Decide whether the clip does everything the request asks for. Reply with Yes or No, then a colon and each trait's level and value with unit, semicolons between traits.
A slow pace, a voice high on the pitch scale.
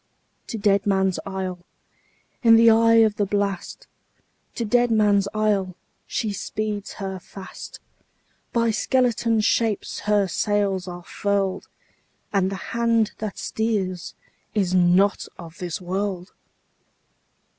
Yes: slow, 115 wpm; high, 205 Hz